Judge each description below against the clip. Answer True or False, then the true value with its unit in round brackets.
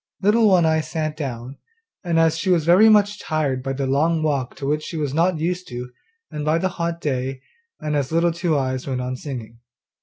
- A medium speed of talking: False (210 wpm)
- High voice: False (155 Hz)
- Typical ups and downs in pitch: True (4.0 semitones)